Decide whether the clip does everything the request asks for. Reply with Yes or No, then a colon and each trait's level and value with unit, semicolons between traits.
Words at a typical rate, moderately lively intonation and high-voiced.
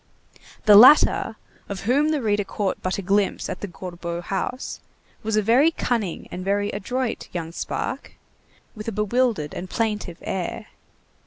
Yes: average, 155 wpm; average, 3.8 semitones; high, 205 Hz